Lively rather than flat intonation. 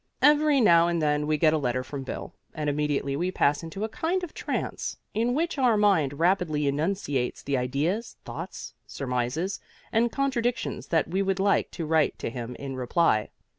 Yes: wide, 6.7 semitones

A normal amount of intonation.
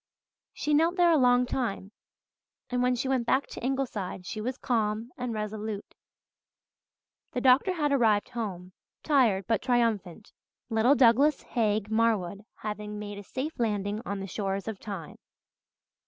Yes: average, 3.7 semitones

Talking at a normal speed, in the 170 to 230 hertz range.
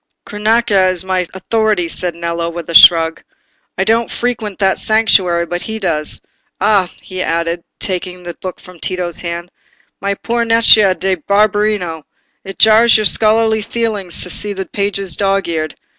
Yes: average, 160 wpm; high, 190 Hz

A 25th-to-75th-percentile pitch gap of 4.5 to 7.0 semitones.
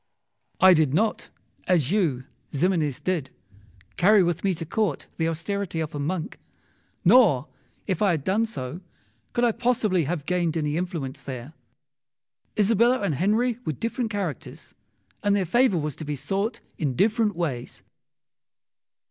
Yes: wide, 5.4 semitones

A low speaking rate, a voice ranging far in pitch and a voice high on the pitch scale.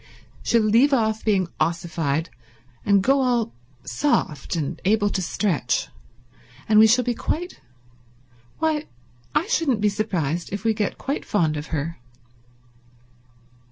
Yes: slow, 125 wpm; wide, 6.8 semitones; high, 205 Hz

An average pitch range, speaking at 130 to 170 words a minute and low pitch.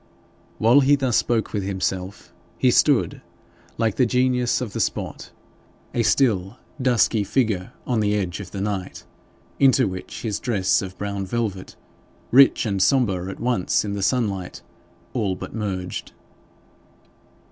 Yes: average, 4.3 semitones; average, 145 wpm; low, 105 Hz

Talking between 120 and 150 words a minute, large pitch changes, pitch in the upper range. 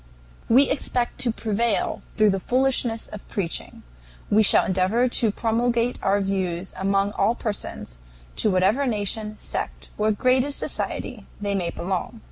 No: average, 145 wpm; average, 3.5 semitones; high, 215 Hz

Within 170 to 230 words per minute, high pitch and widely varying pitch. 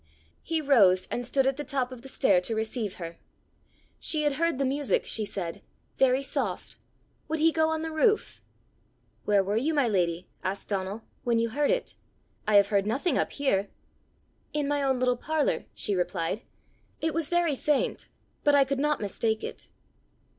Yes: average, 180 wpm; very high, 260 Hz; wide, 6.4 semitones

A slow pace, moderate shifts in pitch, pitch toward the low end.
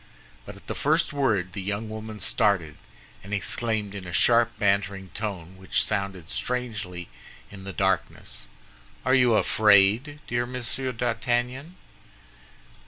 Yes: slow, 130 wpm; average, 3.8 semitones; low, 105 Hz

